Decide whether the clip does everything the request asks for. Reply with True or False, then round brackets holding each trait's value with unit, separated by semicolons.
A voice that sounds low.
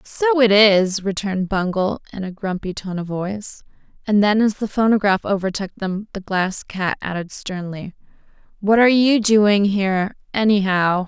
False (200 Hz)